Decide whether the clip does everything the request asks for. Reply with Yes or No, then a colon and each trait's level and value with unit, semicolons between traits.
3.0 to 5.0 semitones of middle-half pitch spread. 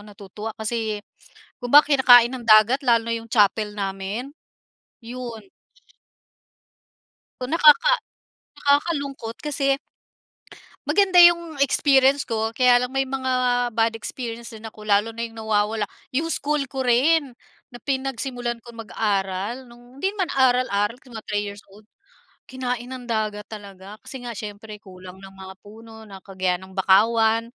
Yes: average, 3.8 semitones